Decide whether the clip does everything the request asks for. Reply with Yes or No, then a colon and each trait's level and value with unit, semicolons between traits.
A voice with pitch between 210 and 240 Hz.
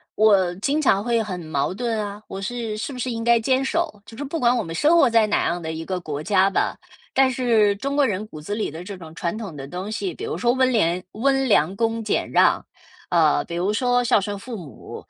Yes: high, 215 Hz